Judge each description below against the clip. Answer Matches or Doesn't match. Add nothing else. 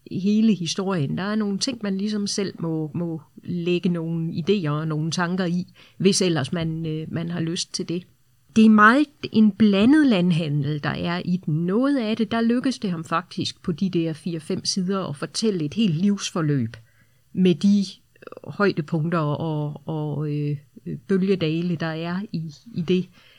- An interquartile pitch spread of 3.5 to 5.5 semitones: Matches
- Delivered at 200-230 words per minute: Doesn't match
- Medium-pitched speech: Matches